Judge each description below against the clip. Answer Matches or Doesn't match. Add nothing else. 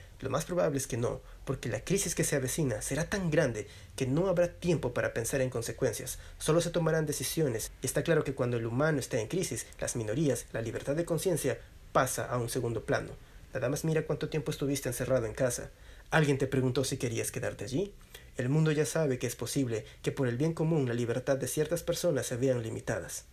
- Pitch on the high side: Doesn't match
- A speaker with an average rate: Doesn't match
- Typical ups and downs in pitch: Matches